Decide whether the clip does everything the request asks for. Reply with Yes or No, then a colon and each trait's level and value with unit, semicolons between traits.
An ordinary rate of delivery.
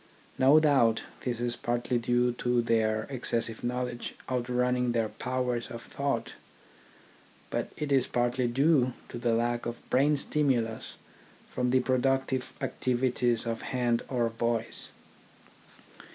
No: slow, 125 wpm